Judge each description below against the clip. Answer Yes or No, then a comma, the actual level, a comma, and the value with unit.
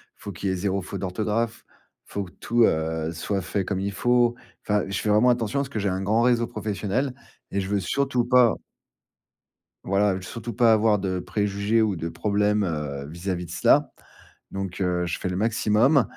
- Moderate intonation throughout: Yes, average, 3.5 semitones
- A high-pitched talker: No, low, 100 Hz